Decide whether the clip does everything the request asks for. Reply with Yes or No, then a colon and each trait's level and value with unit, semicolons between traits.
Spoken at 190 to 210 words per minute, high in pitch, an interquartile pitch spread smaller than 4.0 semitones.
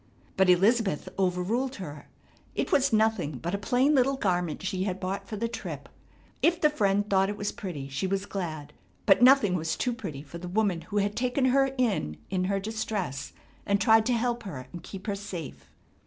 No: average, 200 wpm; high, 200 Hz; average, 4.4 semitones